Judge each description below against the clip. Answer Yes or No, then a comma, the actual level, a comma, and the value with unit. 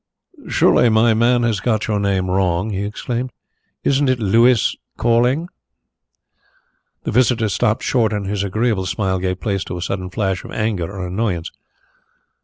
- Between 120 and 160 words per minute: Yes, average, 155 wpm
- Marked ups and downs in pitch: No, average, 3.7 semitones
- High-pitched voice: No, low, 105 Hz